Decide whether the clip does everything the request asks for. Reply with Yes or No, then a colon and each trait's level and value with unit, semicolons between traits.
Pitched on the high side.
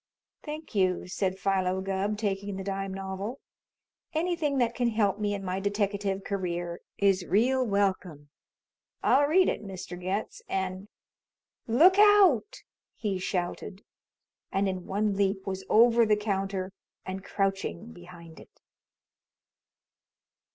Yes: high, 195 Hz